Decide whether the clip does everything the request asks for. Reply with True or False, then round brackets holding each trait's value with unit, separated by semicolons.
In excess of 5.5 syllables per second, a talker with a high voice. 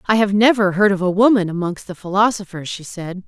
True (5.7 syllables/s; 195 Hz)